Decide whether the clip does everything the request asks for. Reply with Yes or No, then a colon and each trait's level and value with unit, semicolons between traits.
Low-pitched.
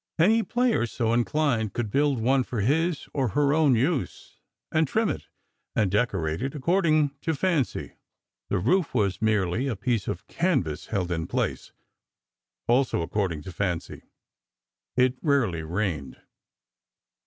Yes: low, 125 Hz